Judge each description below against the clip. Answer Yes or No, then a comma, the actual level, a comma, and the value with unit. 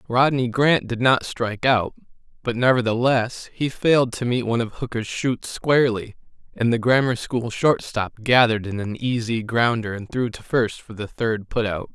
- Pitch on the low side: Yes, low, 120 Hz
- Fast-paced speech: No, average, 180 wpm